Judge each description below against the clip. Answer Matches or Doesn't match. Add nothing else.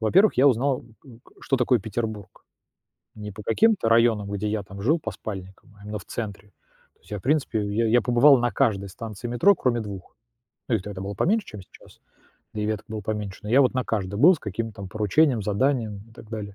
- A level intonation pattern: Doesn't match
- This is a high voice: Doesn't match